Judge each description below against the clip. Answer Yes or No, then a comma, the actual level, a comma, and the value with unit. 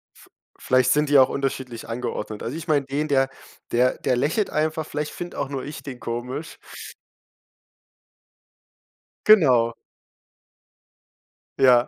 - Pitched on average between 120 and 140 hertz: Yes, low, 135 Hz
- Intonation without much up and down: No, average, 3.3 semitones